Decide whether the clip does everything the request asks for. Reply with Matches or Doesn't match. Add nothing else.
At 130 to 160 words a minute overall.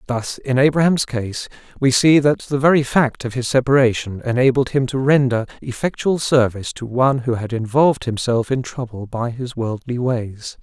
Doesn't match